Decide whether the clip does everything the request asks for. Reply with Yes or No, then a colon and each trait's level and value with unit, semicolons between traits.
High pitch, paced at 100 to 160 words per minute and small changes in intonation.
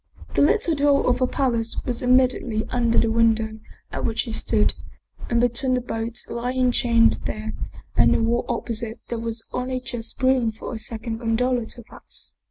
No: high, 235 Hz; average, 180 wpm; narrow, 1.8 semitones